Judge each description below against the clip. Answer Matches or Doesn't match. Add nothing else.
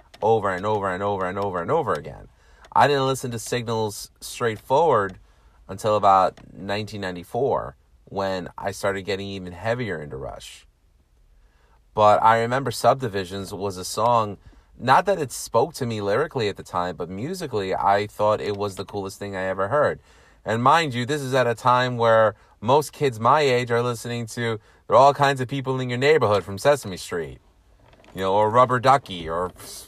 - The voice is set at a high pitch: Doesn't match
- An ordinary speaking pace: Matches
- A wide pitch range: Doesn't match